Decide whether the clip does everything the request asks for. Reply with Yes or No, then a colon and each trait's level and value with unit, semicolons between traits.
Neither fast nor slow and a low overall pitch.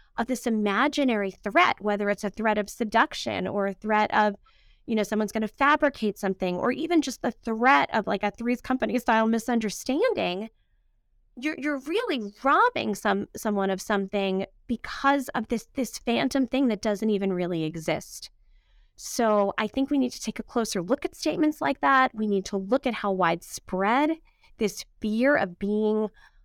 No: average, 170 wpm; high, 220 Hz